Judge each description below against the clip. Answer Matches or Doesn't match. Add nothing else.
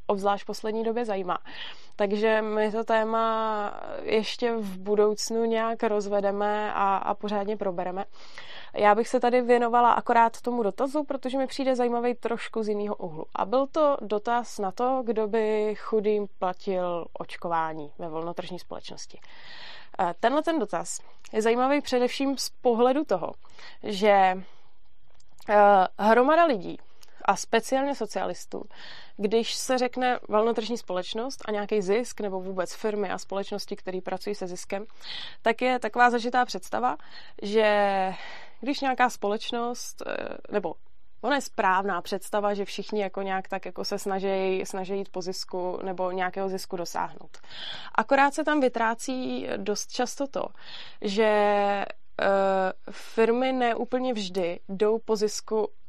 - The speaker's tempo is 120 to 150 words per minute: Matches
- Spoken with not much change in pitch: Doesn't match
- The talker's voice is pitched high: Matches